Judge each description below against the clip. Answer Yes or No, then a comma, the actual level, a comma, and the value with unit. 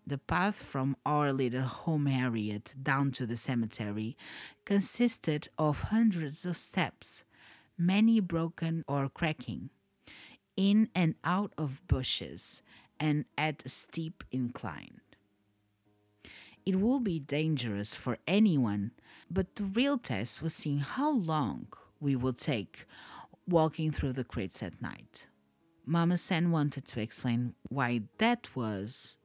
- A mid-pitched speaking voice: Yes, medium, 145 Hz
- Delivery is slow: Yes, slow, 125 wpm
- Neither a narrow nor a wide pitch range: No, wide, 5.9 semitones